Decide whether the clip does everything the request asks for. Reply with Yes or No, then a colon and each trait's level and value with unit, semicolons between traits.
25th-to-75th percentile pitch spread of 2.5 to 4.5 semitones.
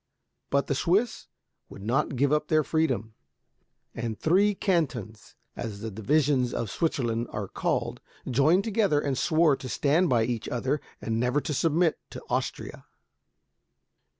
No: wide, 5.5 semitones